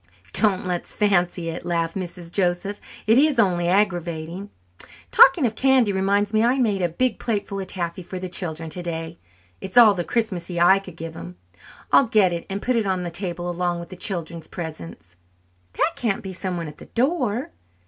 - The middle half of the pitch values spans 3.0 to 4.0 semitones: Yes, average, 3.4 semitones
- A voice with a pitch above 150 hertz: Yes, medium, 185 Hz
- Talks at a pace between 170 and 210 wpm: Yes, average, 195 wpm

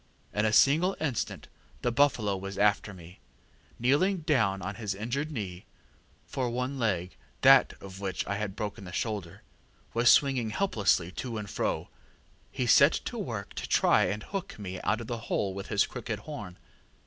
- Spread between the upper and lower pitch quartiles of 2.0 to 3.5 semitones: No, average, 4.5 semitones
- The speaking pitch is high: No, low, 105 Hz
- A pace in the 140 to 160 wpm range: No, average, 170 wpm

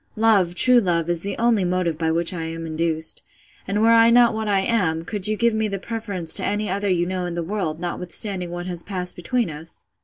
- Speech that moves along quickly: Yes, fast, 235 wpm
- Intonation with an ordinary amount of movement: Yes, average, 4.1 semitones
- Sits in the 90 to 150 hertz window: No, medium, 185 Hz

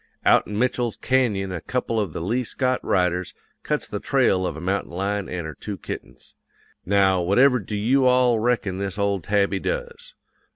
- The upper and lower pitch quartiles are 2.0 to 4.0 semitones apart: No, average, 5.0 semitones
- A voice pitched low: Yes, low, 105 Hz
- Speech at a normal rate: Yes, average, 180 wpm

